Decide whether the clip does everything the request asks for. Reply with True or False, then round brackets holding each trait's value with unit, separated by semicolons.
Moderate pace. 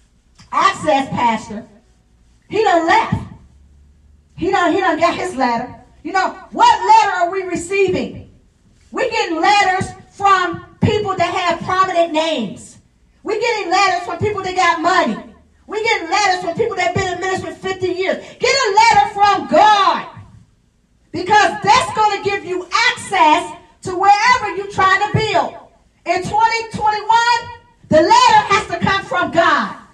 True (150 wpm)